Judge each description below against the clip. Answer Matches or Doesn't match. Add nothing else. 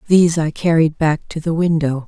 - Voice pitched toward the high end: Doesn't match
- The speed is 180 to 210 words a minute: Matches